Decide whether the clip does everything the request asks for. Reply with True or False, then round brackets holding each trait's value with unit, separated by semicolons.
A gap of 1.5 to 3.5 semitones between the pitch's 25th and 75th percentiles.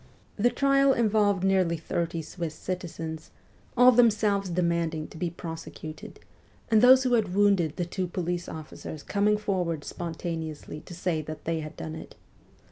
False (4.1 semitones)